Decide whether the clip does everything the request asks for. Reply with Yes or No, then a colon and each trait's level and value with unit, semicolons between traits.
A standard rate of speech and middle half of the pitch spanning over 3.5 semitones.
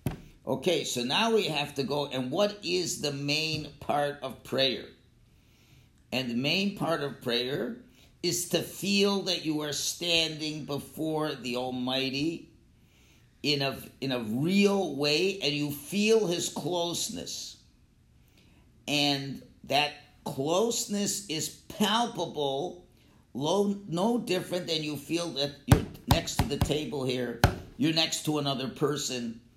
No: slow, 130 wpm; average, 4.2 semitones